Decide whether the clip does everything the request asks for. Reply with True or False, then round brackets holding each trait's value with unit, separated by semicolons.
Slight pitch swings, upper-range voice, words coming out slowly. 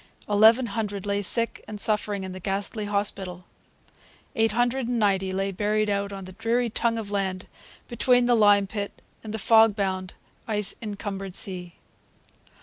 False (2.3 semitones; 205 Hz; 160 wpm)